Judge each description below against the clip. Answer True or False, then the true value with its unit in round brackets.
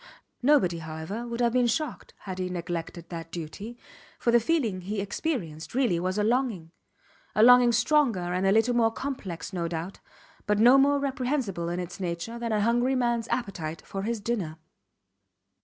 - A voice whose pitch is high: True (215 Hz)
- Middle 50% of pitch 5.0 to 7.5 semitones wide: True (5.5 semitones)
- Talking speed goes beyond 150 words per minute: True (175 wpm)